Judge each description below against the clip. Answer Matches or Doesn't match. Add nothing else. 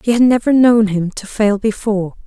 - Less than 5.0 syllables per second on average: Doesn't match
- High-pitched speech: Matches